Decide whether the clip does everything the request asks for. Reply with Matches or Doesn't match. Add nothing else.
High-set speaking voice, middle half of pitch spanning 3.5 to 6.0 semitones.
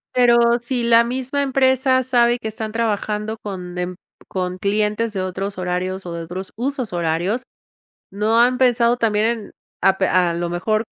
Matches